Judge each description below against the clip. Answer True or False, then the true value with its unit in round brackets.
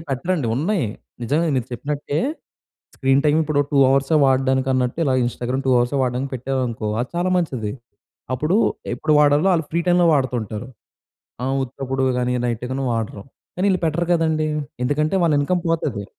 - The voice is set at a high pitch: False (135 Hz)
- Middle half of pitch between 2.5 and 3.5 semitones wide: False (4.1 semitones)